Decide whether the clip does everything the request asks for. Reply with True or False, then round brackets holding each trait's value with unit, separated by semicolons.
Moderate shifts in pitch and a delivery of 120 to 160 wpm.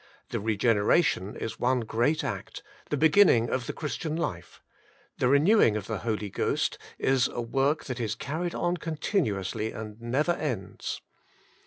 False (5.9 semitones; 150 wpm)